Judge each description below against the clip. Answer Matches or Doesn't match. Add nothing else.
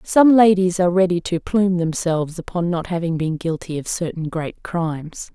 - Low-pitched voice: Doesn't match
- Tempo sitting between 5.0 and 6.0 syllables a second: Matches